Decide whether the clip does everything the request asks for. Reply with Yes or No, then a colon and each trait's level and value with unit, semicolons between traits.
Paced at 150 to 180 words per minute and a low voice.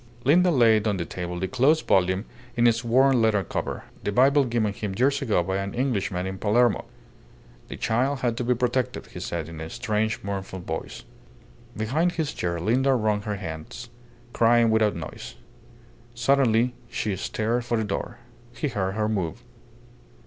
Yes: average, 170 wpm; low, 110 Hz